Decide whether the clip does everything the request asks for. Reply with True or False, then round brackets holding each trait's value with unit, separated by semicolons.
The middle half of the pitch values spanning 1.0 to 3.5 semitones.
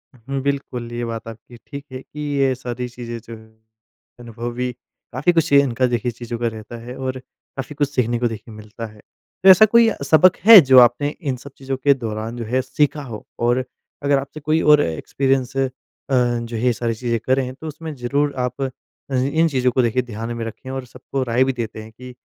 True (2.8 semitones)